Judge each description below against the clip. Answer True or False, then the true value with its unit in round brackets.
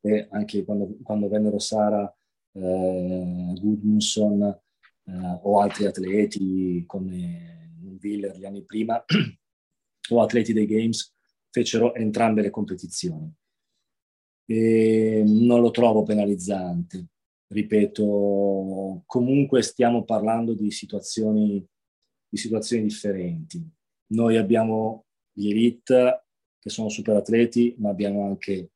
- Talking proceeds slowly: True (105 wpm)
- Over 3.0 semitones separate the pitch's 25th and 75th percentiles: False (2.4 semitones)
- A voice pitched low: True (105 Hz)